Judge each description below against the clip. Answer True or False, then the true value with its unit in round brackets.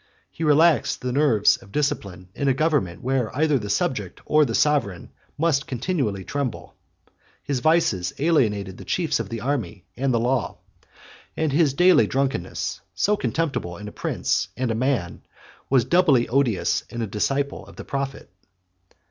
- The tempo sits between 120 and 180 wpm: True (160 wpm)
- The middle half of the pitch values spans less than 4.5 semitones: False (5.5 semitones)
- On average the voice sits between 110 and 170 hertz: True (135 Hz)